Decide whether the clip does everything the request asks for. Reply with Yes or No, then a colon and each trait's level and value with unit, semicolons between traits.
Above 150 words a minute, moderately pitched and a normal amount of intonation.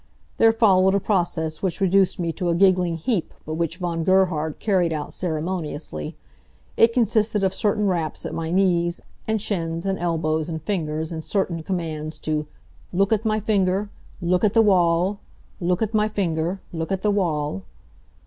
Yes: average, 170 wpm; medium, 180 Hz; average, 3.5 semitones